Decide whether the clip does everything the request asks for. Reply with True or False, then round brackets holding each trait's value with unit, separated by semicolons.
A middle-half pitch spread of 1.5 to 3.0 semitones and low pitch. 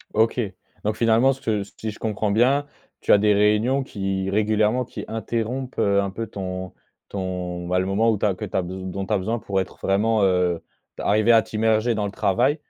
True (2.7 semitones; 105 Hz)